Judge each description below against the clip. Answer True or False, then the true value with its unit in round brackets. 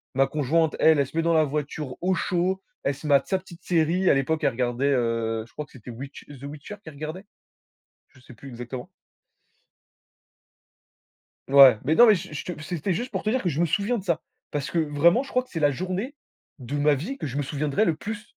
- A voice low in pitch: False (155 Hz)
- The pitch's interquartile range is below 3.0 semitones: False (4.8 semitones)